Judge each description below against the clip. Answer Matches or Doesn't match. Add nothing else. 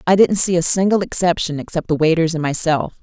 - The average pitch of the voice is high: Doesn't match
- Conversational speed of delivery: Doesn't match